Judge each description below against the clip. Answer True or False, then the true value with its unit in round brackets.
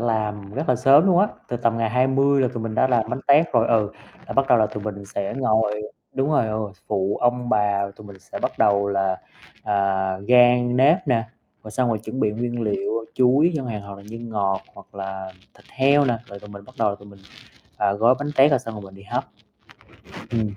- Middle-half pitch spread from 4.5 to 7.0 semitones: False (3.8 semitones)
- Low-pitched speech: True (115 Hz)